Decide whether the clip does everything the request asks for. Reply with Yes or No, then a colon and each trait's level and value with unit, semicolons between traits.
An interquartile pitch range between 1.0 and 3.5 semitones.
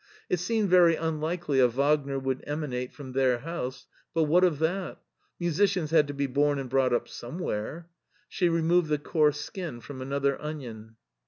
No: average, 3.9 semitones